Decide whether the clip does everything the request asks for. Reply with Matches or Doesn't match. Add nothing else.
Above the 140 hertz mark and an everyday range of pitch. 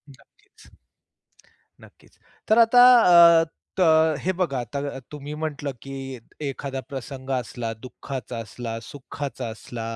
Doesn't match